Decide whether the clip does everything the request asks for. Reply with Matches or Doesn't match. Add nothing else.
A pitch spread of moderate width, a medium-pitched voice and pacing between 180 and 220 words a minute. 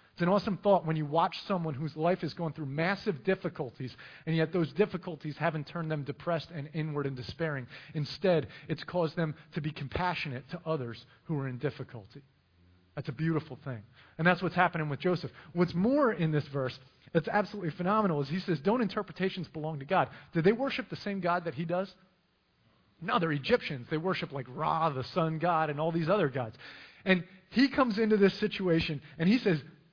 Matches